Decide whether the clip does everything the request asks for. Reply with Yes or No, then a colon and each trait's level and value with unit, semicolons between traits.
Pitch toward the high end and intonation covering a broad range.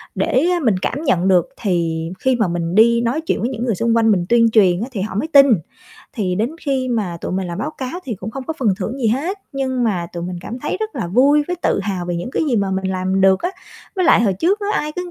Yes: high, 225 Hz; wide, 6.2 semitones